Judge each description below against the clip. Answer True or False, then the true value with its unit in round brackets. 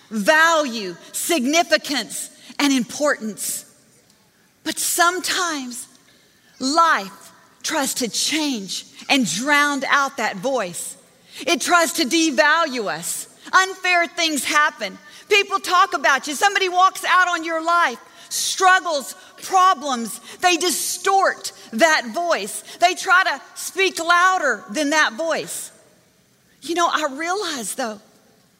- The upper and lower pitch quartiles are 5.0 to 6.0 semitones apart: True (5.3 semitones)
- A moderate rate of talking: False (110 wpm)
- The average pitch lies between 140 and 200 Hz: False (310 Hz)